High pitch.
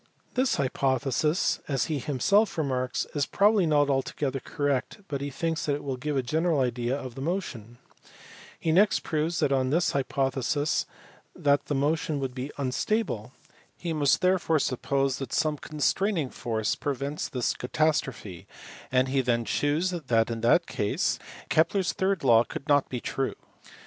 No: medium, 140 Hz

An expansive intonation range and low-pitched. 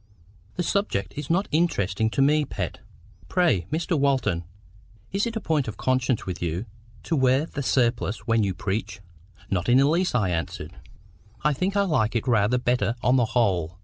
Yes: wide, 7.1 semitones; low, 125 Hz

